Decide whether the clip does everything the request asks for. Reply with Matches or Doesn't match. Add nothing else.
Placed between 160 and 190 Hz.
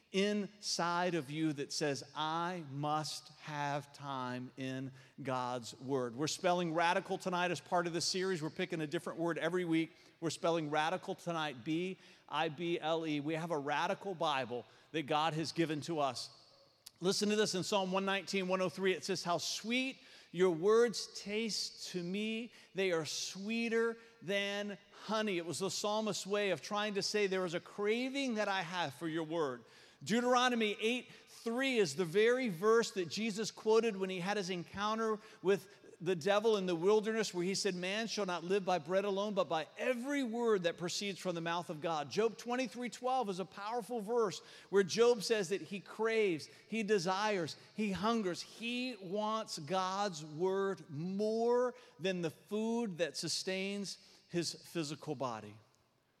Matches